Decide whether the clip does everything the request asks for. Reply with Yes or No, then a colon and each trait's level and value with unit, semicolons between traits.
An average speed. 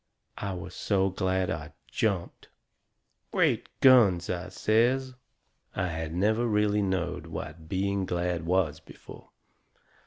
No: slow, 120 wpm